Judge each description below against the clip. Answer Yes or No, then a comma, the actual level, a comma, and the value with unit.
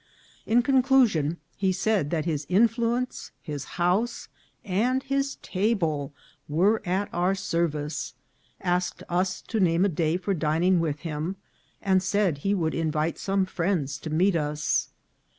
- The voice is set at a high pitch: No, medium, 180 Hz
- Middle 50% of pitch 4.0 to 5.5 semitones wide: Yes, average, 4.3 semitones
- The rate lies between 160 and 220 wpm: No, average, 140 wpm